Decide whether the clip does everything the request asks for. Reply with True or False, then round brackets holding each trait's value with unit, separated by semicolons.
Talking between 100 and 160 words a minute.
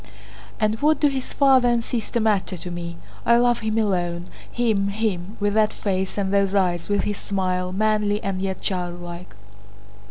False (170 wpm)